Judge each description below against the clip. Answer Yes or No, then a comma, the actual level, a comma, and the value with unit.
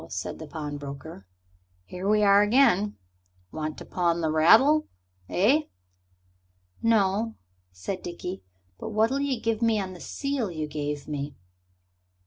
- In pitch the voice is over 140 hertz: Yes, high, 190 Hz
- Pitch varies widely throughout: Yes, wide, 6.4 semitones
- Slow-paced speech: Yes, slow, 130 wpm